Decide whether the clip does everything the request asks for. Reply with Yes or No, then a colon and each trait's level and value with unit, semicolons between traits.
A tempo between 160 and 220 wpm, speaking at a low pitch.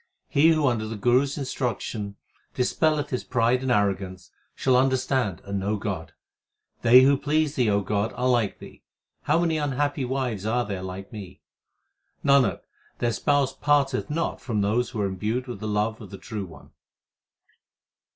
Yes: average, 170 wpm; low, 120 Hz